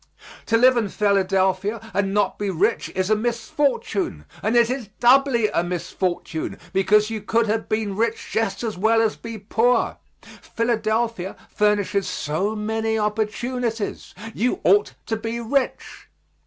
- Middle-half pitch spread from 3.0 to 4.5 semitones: No, narrow, 2.5 semitones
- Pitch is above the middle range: Yes, high, 220 Hz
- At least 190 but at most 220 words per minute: No, average, 140 wpm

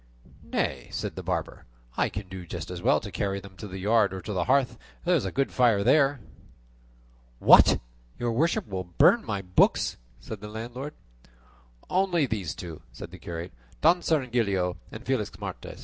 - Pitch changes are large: Yes, wide, 5.8 semitones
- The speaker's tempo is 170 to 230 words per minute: Yes, average, 180 wpm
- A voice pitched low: Yes, low, 105 Hz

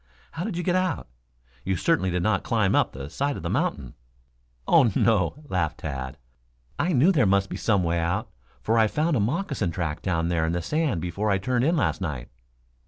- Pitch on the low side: Yes, low, 100 Hz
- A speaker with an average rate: No, fast, 210 wpm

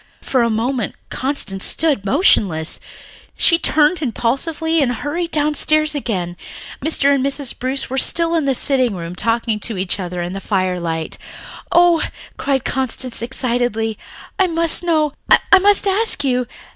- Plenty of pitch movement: Yes, wide, 5.9 semitones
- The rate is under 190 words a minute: Yes, average, 150 wpm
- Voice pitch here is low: No, very high, 265 Hz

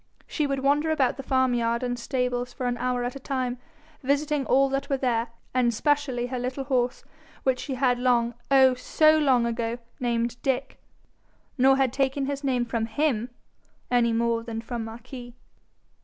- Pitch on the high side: Yes, very high, 250 Hz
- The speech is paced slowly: No, average, 170 wpm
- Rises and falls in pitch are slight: Yes, narrow, 2.1 semitones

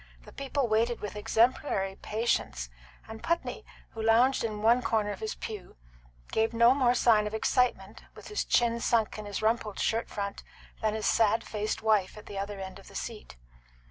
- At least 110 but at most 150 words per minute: No, average, 185 wpm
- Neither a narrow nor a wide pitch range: No, narrow, 2.1 semitones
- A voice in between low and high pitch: No, high, 220 Hz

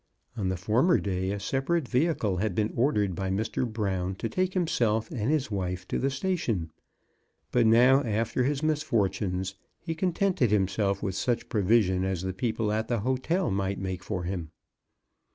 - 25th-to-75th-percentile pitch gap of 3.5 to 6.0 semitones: Yes, wide, 5.6 semitones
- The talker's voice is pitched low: Yes, low, 110 Hz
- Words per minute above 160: Yes, average, 170 wpm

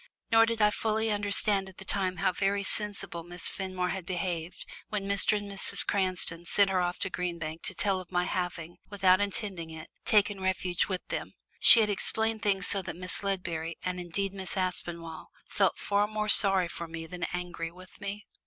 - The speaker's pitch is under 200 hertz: Yes, high, 190 Hz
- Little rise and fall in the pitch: Yes, narrow, 2.3 semitones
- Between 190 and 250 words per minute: Yes, average, 195 wpm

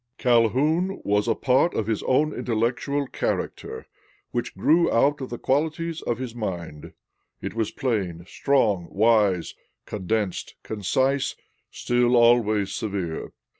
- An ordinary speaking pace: No, slow, 125 wpm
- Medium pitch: No, low, 115 Hz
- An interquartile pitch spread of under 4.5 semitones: No, average, 4.8 semitones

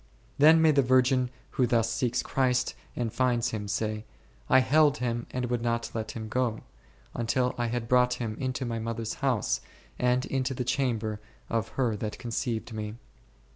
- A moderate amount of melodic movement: No, narrow, 2.2 semitones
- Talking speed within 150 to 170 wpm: No, average, 180 wpm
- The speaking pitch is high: No, low, 120 Hz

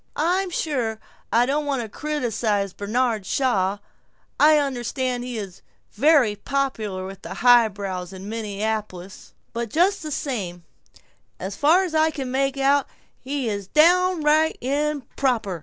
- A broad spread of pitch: Yes, wide, 6.1 semitones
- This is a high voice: Yes, very high, 250 Hz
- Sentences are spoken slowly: Yes, slow, 130 wpm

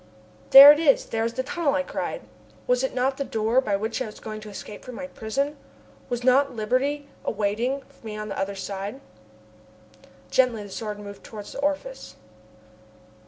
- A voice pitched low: No, high, 245 Hz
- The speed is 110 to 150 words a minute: No, average, 180 wpm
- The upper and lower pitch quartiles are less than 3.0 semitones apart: No, average, 4.5 semitones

